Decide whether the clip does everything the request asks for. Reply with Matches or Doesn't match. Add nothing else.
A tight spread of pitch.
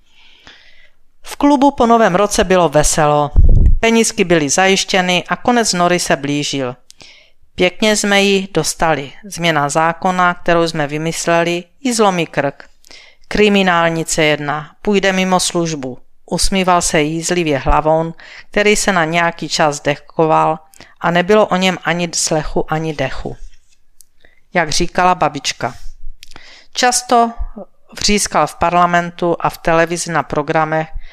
Doesn't match